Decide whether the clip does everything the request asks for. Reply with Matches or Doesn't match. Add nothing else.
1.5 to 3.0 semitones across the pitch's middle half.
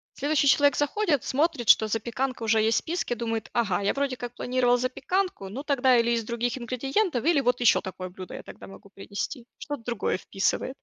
Doesn't match